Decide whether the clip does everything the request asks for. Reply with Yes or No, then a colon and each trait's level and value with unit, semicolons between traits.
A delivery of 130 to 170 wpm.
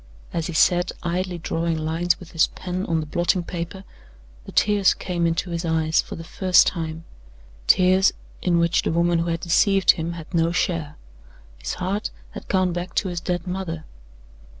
No: average, 180 wpm